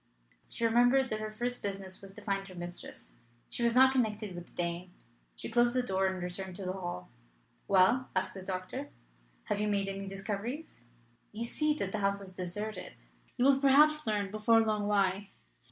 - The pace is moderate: Yes, average, 190 wpm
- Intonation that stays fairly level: No, average, 3.8 semitones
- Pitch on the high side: Yes, high, 205 Hz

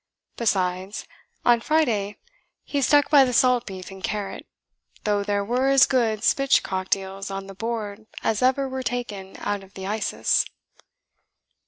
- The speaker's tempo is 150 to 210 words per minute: Yes, average, 155 wpm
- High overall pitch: Yes, high, 215 Hz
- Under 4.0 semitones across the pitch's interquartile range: No, average, 4.4 semitones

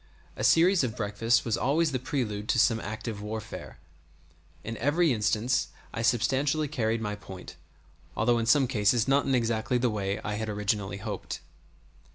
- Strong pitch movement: No, average, 3.6 semitones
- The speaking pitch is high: No, low, 115 Hz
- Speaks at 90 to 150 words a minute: No, average, 175 wpm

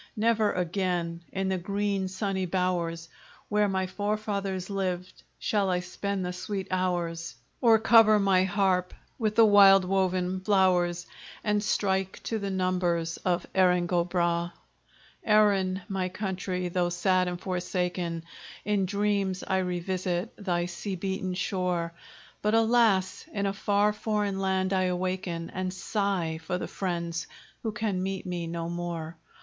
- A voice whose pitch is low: No, medium, 185 Hz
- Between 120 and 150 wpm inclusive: Yes, average, 145 wpm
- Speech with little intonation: Yes, narrow, 2.0 semitones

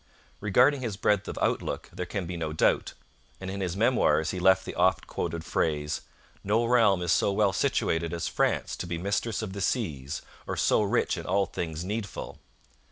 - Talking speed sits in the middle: Yes, average, 190 wpm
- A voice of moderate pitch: No, very low, 95 Hz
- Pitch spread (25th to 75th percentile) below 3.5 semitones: No, average, 3.8 semitones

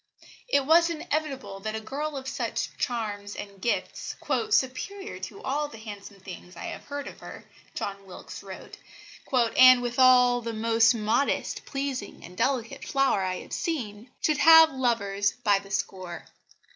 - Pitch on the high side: Yes, high, 240 Hz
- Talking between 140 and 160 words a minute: Yes, average, 155 wpm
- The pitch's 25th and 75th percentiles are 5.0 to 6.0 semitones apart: Yes, wide, 5.4 semitones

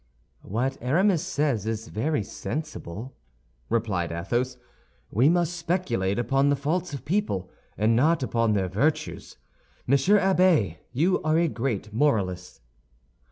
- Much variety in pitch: Yes, wide, 6.7 semitones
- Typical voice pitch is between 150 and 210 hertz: No, low, 130 Hz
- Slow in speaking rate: Yes, slow, 125 wpm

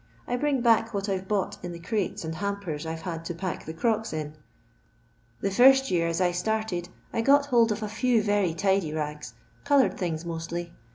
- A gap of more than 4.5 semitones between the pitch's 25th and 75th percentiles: Yes, average, 5.1 semitones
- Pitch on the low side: No, high, 190 Hz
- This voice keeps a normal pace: No, fast, 210 wpm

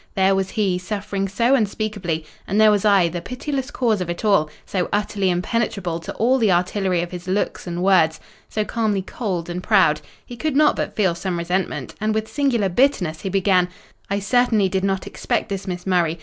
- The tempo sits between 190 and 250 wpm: Yes, average, 195 wpm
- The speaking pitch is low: No, high, 195 Hz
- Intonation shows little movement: No, average, 3.4 semitones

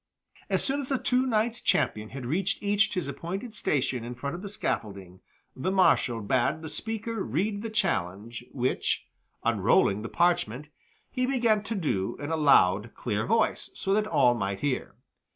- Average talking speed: Yes, average, 170 wpm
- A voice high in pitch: No, medium, 160 Hz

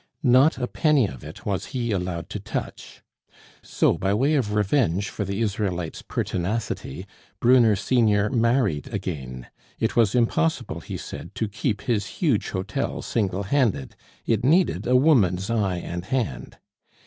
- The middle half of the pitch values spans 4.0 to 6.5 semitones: Yes, average, 4.9 semitones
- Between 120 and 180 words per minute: Yes, average, 150 wpm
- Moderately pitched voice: No, low, 105 Hz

